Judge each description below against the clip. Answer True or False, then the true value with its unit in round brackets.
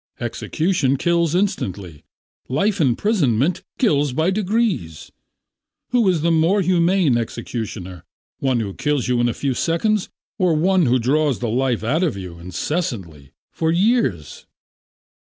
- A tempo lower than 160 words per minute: True (135 wpm)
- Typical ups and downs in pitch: False (7.5 semitones)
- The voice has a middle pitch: True (150 Hz)